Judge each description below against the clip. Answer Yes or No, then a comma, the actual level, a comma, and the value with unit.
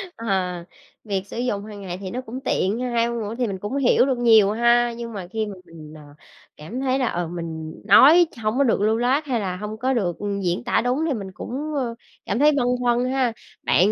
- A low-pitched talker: No, high, 230 Hz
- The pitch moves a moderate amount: Yes, average, 4.2 semitones